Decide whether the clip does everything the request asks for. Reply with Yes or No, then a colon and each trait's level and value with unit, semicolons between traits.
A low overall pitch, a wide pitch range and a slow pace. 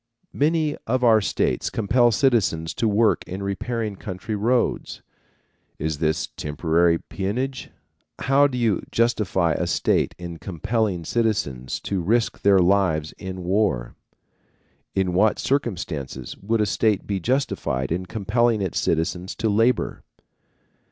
No: low, 100 Hz; average, 5.0 semitones; slow, 130 wpm